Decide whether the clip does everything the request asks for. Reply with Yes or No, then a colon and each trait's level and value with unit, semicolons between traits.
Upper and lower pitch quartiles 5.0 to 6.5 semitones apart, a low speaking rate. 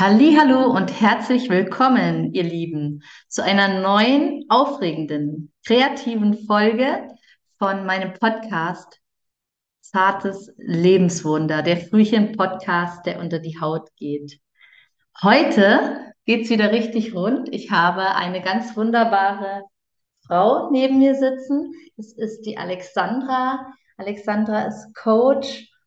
Yes: average, 5.3 semitones; slow, 105 wpm